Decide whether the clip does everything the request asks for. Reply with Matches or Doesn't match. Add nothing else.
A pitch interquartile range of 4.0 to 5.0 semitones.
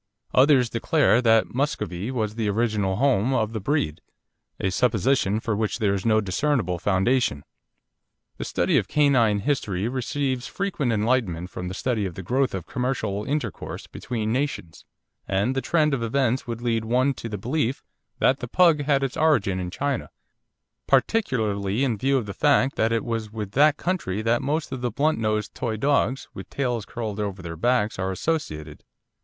Matches